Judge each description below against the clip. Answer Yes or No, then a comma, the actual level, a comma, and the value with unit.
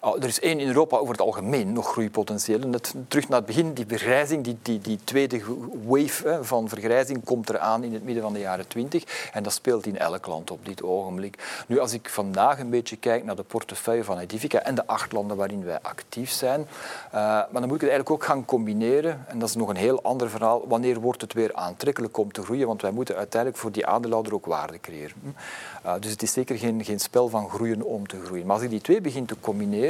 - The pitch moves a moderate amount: Yes, average, 3.0 semitones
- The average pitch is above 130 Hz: No, low, 115 Hz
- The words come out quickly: Yes, fast, 240 wpm